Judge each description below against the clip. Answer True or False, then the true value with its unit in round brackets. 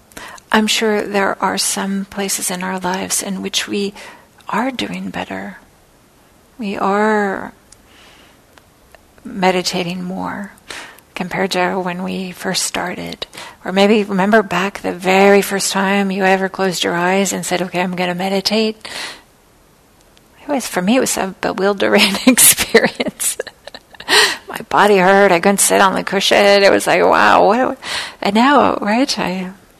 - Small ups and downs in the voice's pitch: True (1.8 semitones)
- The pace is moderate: True (145 wpm)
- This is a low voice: False (195 Hz)